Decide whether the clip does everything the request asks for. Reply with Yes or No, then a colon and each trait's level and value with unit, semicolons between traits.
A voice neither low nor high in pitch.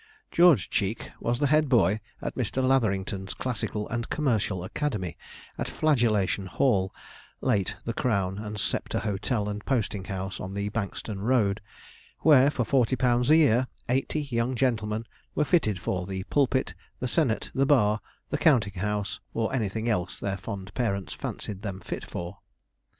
No: low, 110 Hz